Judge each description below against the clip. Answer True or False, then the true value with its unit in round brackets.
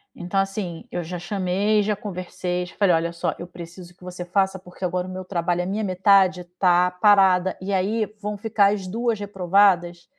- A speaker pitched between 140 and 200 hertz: True (185 Hz)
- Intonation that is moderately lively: False (2.1 semitones)